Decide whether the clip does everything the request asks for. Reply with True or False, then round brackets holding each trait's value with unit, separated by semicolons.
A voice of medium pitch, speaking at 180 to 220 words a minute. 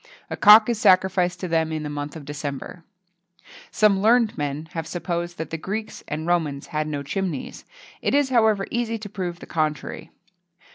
True (175 Hz; 185 wpm)